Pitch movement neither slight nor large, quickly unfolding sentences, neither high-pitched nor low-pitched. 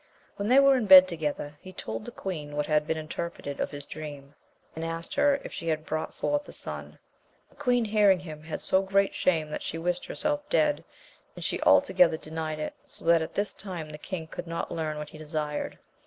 Yes: average, 4.1 semitones; fast, 215 wpm; medium, 165 Hz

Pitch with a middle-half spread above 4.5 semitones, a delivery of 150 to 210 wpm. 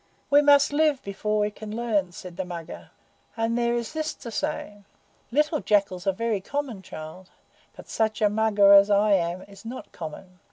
No: average, 3.7 semitones; average, 185 wpm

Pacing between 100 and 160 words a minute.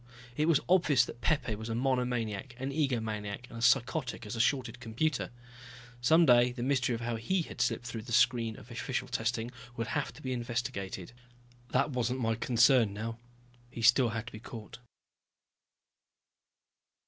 No: average, 170 wpm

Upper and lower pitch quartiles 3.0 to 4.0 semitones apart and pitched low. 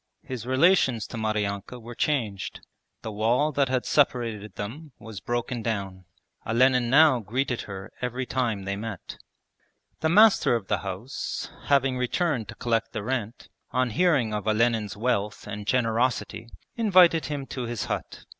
Yes: average, 3.6 semitones; low, 120 Hz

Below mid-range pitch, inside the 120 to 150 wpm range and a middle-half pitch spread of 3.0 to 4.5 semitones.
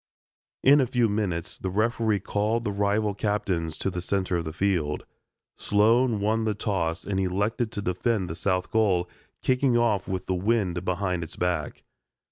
No: low, 100 Hz; average, 170 wpm; average, 3.4 semitones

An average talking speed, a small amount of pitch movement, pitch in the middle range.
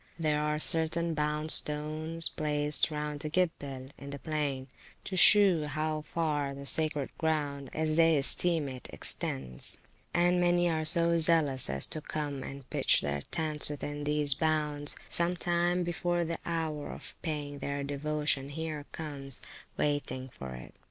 Yes: average, 150 wpm; narrow, 2.2 semitones; medium, 150 Hz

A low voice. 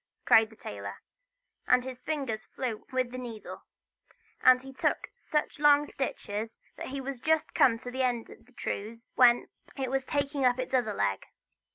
No: very high, 255 Hz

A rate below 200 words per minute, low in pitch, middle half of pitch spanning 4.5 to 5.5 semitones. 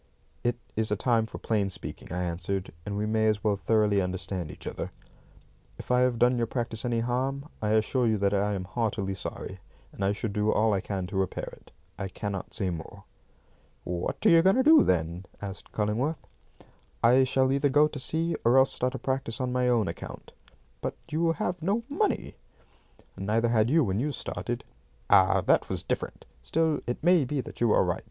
No: fast, 205 wpm; low, 110 Hz; average, 4.9 semitones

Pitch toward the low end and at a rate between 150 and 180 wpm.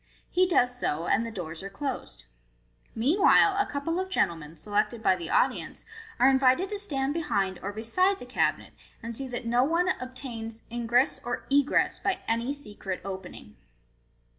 No: high, 245 Hz; average, 165 wpm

